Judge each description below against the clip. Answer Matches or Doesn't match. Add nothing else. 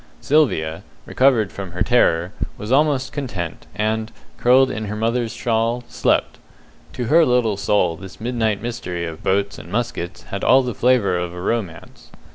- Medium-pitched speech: Doesn't match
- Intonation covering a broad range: Doesn't match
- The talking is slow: Doesn't match